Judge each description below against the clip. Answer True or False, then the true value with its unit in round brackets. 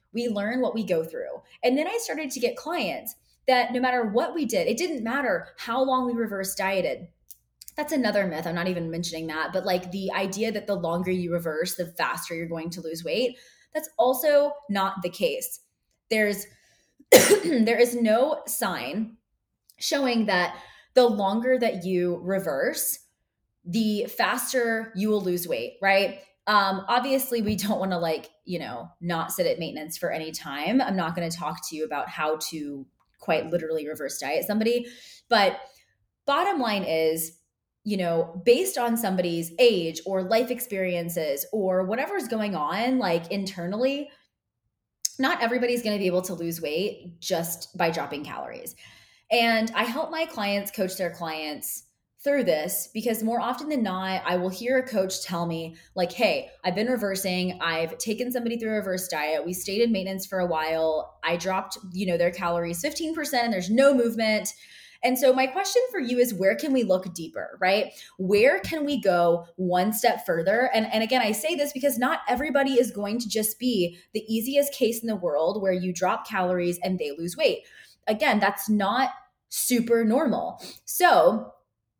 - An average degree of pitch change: False (5.8 semitones)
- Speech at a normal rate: True (180 wpm)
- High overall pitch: True (210 Hz)